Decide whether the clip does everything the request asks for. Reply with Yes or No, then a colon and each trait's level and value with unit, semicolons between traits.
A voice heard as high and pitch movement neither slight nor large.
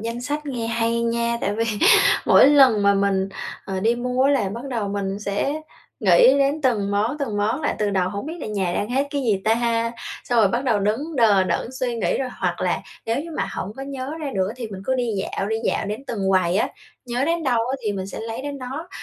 Yes: high, 230 Hz; average, 4.6 semitones